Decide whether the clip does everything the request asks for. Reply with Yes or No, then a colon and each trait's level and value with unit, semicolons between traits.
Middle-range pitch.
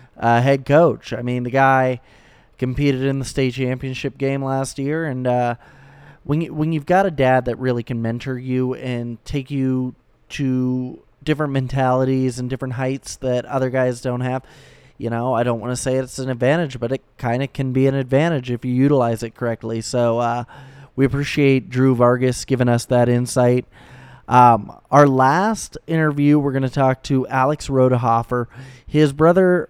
No: low, 130 Hz